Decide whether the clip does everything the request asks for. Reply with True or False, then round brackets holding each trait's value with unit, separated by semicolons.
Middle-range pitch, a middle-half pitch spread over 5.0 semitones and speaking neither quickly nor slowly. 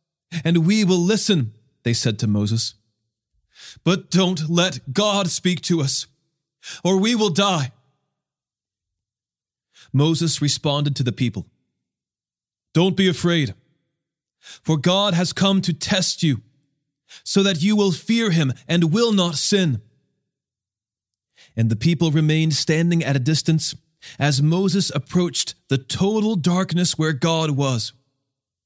False (155 Hz; 5.5 semitones; 130 wpm)